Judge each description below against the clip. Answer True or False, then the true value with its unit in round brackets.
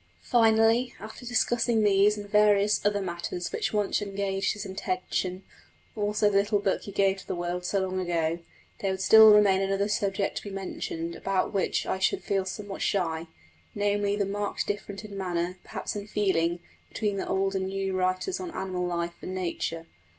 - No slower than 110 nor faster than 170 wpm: False (180 wpm)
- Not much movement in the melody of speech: True (1.9 semitones)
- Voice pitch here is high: True (195 Hz)